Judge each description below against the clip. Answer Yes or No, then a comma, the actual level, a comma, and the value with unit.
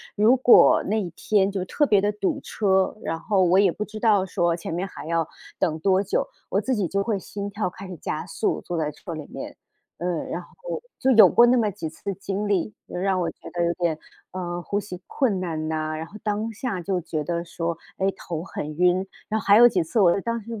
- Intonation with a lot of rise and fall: No, average, 3.5 semitones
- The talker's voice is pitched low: No, high, 190 Hz